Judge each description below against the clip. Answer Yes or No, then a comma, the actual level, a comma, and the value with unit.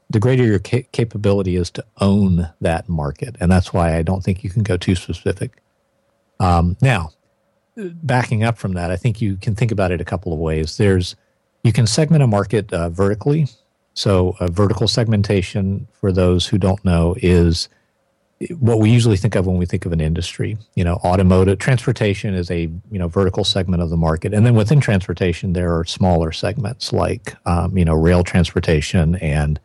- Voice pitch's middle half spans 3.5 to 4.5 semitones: Yes, average, 3.9 semitones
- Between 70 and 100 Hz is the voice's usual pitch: Yes, very low, 95 Hz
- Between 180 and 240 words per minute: Yes, average, 190 wpm